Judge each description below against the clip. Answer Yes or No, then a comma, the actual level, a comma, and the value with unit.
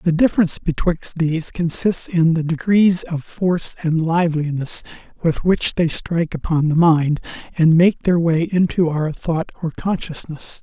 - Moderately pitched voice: Yes, medium, 165 Hz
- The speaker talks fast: No, average, 160 wpm